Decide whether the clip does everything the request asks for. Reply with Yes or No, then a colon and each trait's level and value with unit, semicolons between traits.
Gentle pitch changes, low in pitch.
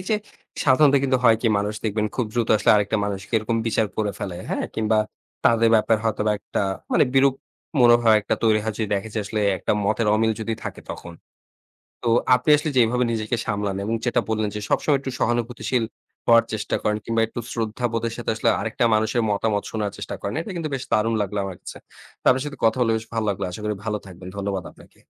Yes: narrow, 2.2 semitones; low, 110 Hz